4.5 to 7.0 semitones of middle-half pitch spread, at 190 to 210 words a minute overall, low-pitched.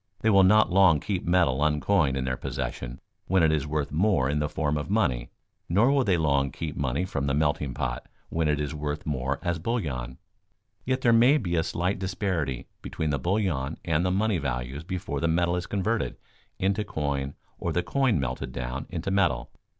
Yes: wide, 5.5 semitones; average, 195 wpm; very low, 80 Hz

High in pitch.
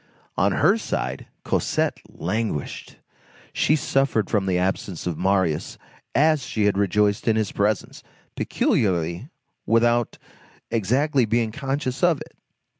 No: low, 110 Hz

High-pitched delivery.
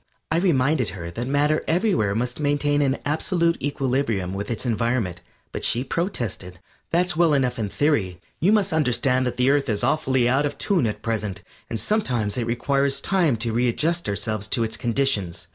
No: low, 130 Hz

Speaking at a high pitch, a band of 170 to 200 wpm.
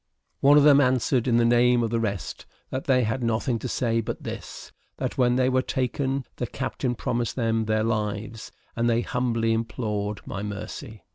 No: low, 120 Hz; average, 190 wpm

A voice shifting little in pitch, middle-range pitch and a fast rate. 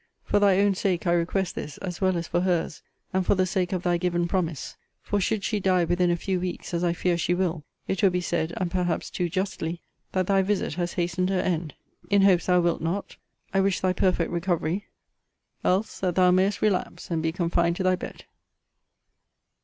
Yes: narrow, 1.7 semitones; medium, 180 Hz; fast, 210 wpm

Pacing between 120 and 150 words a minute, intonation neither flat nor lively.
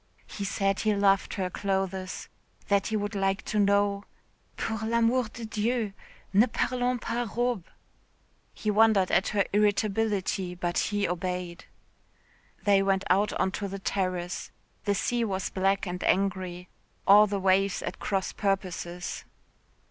No: average, 140 wpm; narrow, 2.1 semitones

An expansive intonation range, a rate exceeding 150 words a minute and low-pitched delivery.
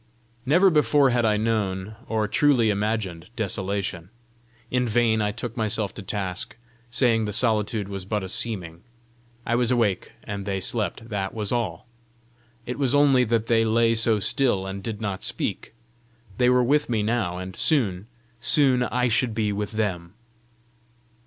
No: average, 3.4 semitones; average, 160 wpm; low, 110 Hz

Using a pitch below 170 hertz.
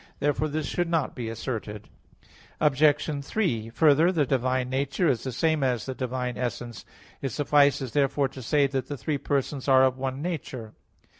Yes: low, 135 Hz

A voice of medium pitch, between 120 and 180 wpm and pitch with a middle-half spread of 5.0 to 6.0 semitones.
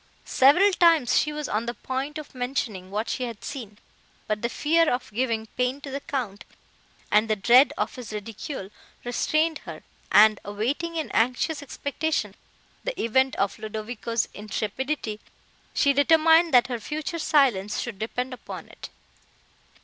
No: very high, 250 Hz; average, 150 wpm; wide, 5.5 semitones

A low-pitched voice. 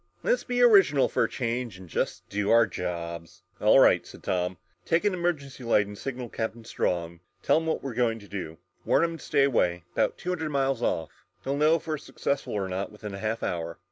Yes: low, 115 Hz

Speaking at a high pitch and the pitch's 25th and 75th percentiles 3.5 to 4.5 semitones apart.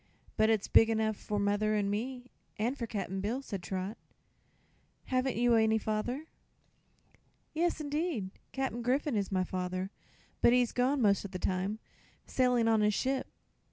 Yes: high, 220 Hz; average, 3.9 semitones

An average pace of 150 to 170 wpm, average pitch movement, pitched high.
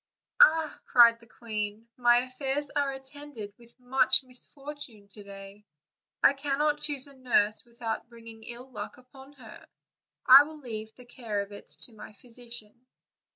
Yes: average, 155 wpm; average, 3.6 semitones; high, 245 Hz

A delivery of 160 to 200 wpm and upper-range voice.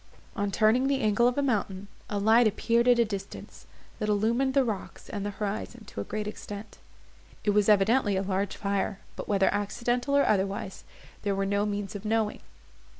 Yes: average, 190 wpm; high, 210 Hz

